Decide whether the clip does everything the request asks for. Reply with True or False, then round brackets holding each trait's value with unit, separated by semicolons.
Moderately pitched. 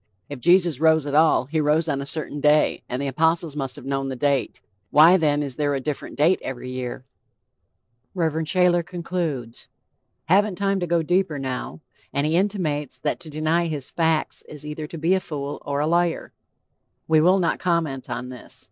True (155 Hz)